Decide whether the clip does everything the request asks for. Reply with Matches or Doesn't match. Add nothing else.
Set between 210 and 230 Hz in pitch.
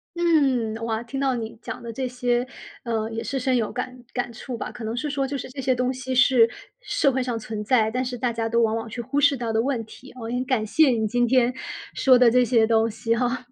Doesn't match